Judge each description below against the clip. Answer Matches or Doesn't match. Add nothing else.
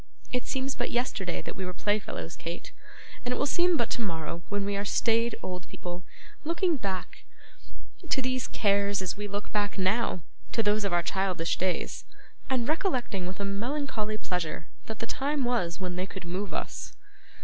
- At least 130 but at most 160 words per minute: Doesn't match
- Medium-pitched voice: Doesn't match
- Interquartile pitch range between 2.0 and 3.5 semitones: Doesn't match